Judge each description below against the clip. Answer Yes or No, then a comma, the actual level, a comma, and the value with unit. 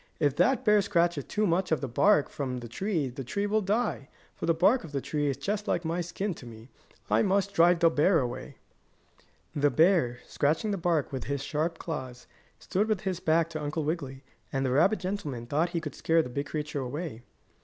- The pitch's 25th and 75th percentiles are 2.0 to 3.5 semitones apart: No, average, 4.9 semitones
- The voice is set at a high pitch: No, medium, 160 Hz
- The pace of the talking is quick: Yes, fast, 220 wpm